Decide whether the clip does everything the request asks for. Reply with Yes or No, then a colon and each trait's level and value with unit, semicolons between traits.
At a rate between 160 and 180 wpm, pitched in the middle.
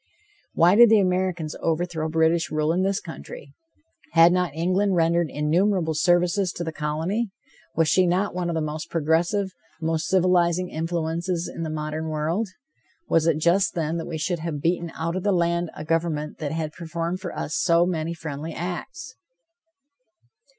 Yes: average, 170 wpm; medium, 170 Hz